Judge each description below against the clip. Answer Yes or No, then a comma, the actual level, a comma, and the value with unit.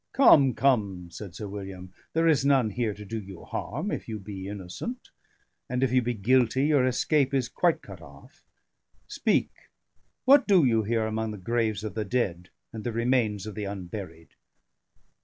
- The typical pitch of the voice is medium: No, low, 110 Hz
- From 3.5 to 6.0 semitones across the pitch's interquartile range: Yes, average, 4.6 semitones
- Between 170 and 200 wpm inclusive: Yes, average, 175 wpm